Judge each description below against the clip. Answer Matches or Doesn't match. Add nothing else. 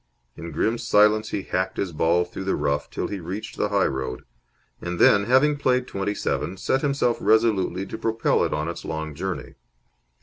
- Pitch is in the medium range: Doesn't match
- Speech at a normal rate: Matches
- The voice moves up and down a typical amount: Matches